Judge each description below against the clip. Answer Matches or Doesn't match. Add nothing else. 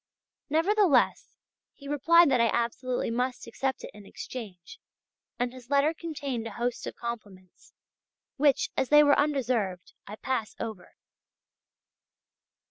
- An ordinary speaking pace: Doesn't match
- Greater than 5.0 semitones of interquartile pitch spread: Doesn't match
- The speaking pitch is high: Matches